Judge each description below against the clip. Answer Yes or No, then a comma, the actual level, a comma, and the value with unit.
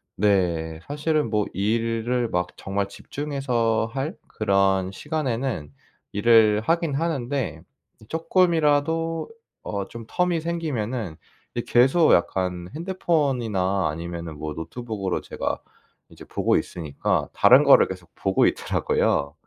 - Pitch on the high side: No, low, 115 Hz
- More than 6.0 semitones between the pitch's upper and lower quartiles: Yes, wide, 7.3 semitones